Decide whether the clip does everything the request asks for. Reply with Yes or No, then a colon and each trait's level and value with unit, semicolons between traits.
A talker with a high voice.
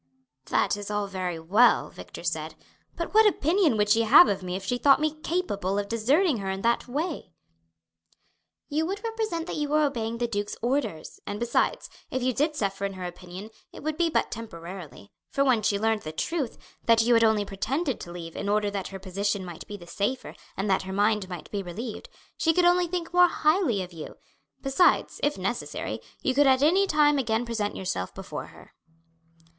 Yes: high, 225 Hz